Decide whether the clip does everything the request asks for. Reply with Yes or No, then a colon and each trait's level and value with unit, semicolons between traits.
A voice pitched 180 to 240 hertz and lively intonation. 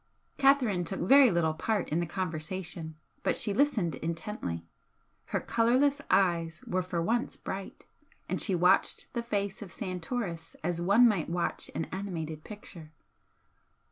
No: medium, 185 Hz; average, 4.5 semitones